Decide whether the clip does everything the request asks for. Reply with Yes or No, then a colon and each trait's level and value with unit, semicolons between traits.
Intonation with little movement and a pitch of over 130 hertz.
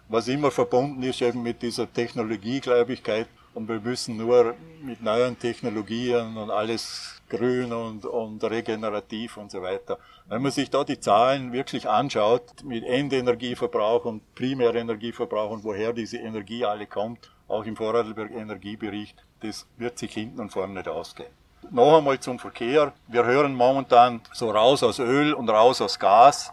No: narrow, 2.0 semitones; low, 120 Hz